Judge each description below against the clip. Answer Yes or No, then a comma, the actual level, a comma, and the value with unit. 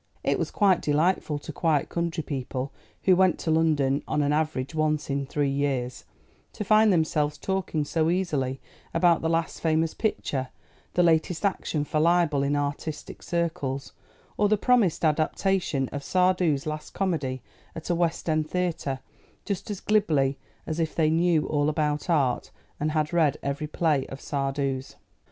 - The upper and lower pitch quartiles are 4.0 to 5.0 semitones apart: No, average, 3.2 semitones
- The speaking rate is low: No, average, 160 wpm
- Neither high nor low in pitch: Yes, medium, 155 Hz